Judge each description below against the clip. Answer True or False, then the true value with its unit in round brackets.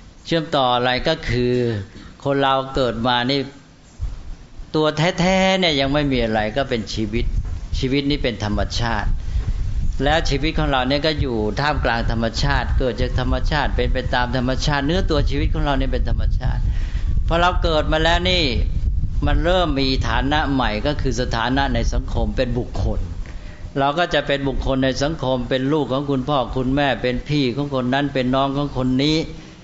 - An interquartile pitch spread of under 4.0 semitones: False (4.6 semitones)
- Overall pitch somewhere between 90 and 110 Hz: False (130 Hz)